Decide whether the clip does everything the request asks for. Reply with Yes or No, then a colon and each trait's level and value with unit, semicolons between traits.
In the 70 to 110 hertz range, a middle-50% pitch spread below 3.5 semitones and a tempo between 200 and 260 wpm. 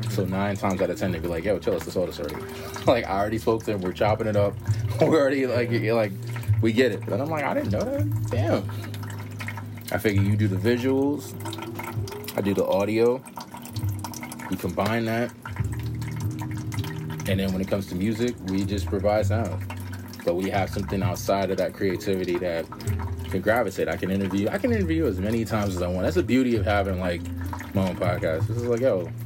Yes: low, 105 Hz; average, 2.8 semitones; fast, 205 wpm